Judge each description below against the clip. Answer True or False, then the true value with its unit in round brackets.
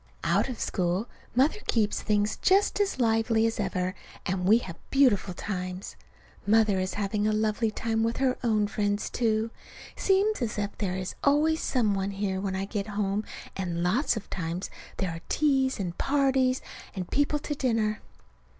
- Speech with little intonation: False (4.7 semitones)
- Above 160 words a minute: True (170 wpm)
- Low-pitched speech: False (215 Hz)